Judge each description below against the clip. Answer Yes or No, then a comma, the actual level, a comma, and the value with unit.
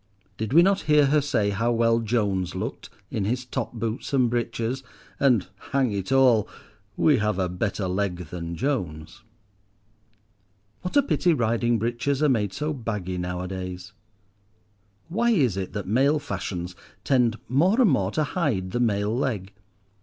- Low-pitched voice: Yes, low, 115 Hz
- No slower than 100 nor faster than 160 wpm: Yes, average, 155 wpm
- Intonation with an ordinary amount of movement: No, wide, 5.9 semitones